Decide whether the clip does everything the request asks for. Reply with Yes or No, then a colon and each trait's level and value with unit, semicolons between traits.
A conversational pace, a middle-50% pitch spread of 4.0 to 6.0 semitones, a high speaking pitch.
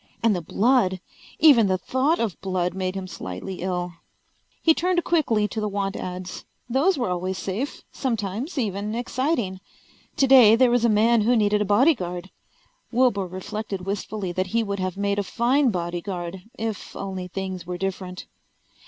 Yes: average, 160 wpm; average, 4.3 semitones; high, 200 Hz